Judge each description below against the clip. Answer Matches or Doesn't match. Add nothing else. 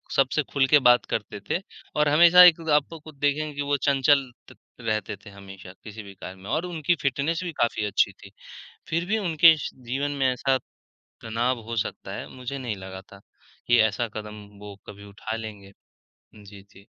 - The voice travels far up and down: Matches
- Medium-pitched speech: Doesn't match